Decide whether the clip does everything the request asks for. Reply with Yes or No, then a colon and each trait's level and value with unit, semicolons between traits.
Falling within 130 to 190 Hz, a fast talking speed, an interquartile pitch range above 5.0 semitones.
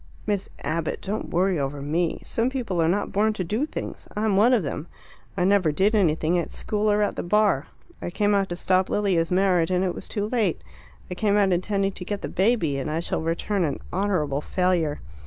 No: medium, 185 Hz; fast, 215 wpm; average, 3.8 semitones